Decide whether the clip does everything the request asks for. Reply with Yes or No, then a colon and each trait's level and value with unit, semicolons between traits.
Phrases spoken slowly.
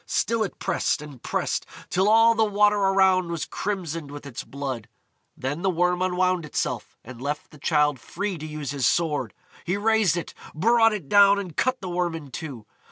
No: average, 190 wpm